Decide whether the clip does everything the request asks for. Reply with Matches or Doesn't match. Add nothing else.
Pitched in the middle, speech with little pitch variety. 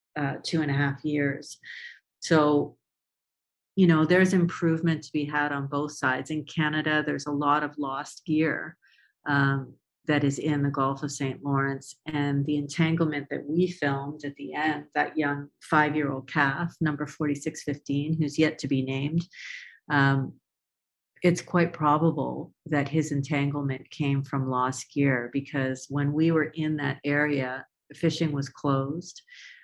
Matches